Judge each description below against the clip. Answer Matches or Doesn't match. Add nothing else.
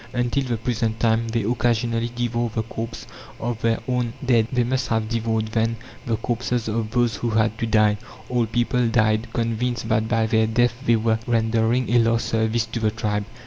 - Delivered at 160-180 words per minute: Doesn't match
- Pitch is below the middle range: Matches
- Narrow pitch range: Matches